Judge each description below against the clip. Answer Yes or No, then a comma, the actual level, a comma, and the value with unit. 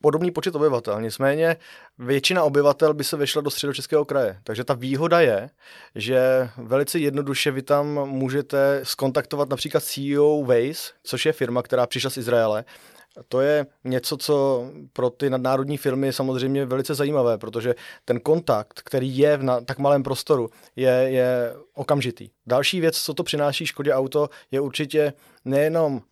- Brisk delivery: No, average, 155 wpm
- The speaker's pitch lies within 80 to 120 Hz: No, medium, 140 Hz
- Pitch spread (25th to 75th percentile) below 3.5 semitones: Yes, narrow, 2.4 semitones